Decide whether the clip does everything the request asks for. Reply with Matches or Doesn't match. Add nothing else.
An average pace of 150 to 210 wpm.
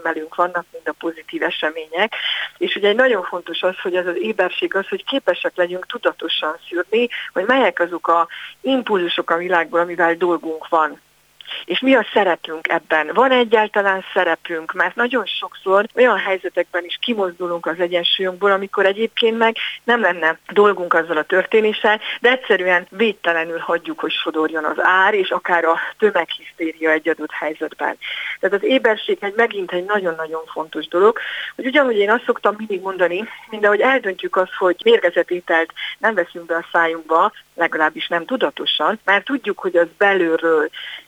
Matches